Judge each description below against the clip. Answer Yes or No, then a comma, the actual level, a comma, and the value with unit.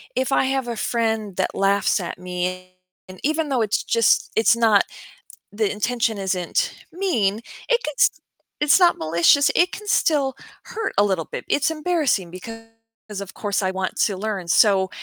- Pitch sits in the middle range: No, high, 220 Hz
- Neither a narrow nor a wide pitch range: No, wide, 6.8 semitones